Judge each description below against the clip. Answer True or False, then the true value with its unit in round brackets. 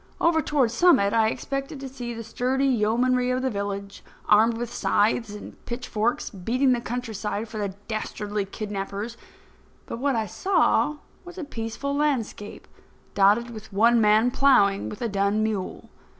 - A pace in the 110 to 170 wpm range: True (155 wpm)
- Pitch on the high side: True (230 Hz)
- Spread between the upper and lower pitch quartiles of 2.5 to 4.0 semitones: True (3.5 semitones)